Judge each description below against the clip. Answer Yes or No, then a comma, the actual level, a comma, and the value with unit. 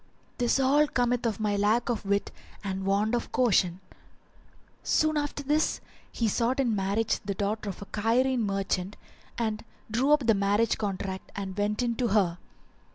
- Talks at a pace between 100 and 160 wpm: No, average, 170 wpm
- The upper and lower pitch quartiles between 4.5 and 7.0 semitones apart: No, average, 3.6 semitones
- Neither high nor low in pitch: No, high, 215 Hz